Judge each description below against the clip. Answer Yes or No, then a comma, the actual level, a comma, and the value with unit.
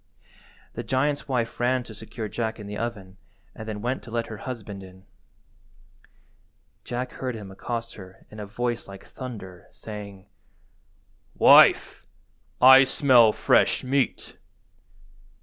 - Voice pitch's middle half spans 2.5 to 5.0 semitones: Yes, average, 3.5 semitones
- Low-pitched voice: Yes, low, 115 Hz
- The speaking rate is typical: No, slow, 130 wpm